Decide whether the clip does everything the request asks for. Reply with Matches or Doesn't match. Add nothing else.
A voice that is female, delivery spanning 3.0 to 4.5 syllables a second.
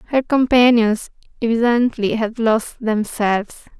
Matches